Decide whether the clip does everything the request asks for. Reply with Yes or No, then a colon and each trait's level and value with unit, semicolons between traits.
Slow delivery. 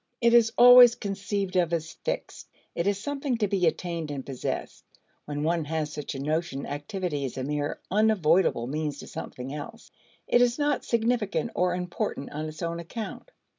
No: average, 175 wpm